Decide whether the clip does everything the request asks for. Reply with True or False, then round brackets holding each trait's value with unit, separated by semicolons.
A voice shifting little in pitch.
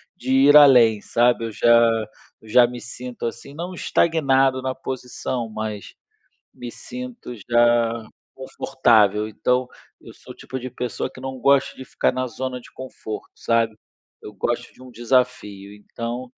True (2.2 semitones)